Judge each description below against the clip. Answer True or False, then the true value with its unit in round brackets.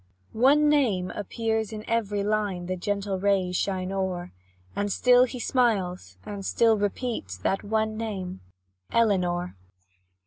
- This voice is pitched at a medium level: False (205 Hz)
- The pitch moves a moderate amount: True (3.3 semitones)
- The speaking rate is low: True (130 wpm)